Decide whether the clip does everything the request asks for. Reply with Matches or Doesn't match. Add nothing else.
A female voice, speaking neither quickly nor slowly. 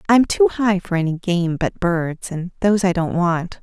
Doesn't match